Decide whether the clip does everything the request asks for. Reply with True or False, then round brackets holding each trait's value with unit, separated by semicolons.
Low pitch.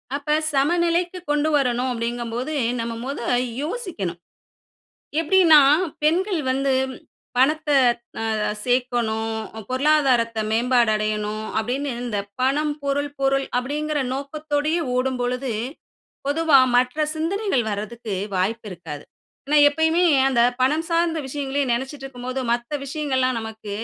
False (270 Hz)